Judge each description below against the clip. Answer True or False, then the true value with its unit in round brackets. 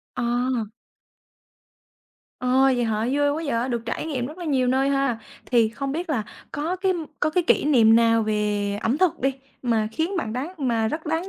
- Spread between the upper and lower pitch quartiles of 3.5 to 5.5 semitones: True (4.9 semitones)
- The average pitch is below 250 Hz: False (260 Hz)